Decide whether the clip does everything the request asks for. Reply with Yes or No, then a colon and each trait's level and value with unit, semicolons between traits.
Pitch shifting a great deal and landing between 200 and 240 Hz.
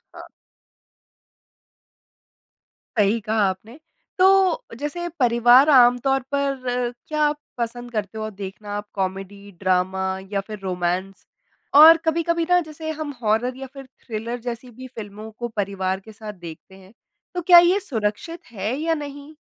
Yes: wide, 6.0 semitones; high, 235 Hz